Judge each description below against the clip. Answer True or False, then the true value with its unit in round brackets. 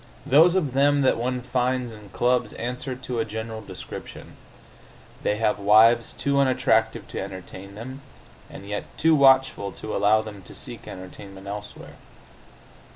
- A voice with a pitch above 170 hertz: False (115 Hz)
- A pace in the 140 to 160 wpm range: True (150 wpm)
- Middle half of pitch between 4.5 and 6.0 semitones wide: False (3.9 semitones)